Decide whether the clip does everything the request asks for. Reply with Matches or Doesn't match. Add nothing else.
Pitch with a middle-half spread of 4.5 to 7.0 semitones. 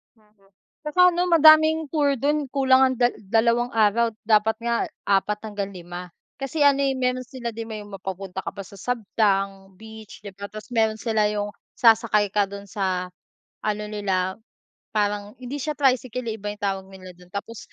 Doesn't match